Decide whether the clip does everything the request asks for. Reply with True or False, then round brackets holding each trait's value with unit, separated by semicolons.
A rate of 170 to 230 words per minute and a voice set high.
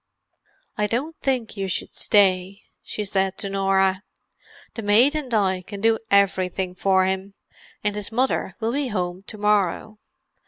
False (150 wpm; 200 Hz)